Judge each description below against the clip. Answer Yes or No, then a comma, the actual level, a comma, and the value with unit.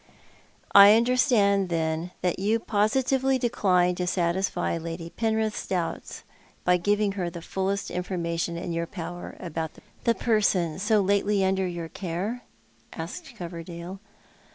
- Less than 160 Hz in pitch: No, medium, 185 Hz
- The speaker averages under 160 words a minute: Yes, slow, 135 wpm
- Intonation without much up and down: No, average, 3.4 semitones